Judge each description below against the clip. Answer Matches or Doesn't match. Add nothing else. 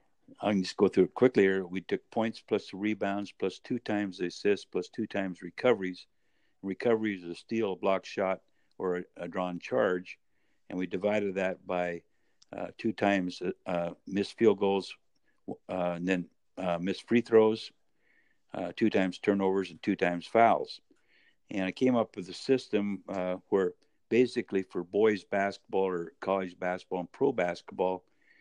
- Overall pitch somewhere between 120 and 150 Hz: Doesn't match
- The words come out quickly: Doesn't match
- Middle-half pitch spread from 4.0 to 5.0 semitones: Doesn't match